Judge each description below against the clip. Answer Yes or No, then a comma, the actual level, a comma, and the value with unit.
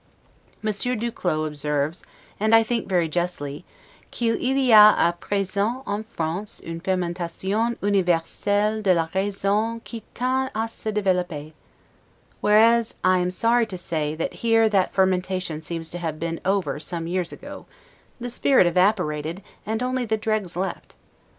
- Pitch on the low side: No, high, 190 Hz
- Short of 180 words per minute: Yes, average, 150 wpm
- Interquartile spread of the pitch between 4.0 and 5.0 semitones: Yes, average, 4.4 semitones